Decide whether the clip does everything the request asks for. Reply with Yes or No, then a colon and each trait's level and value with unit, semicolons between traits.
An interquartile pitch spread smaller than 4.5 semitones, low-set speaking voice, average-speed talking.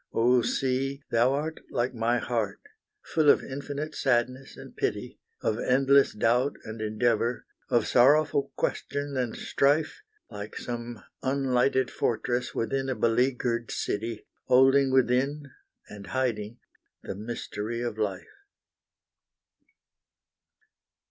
No: average, 2.8 semitones; low, 125 Hz; slow, 110 wpm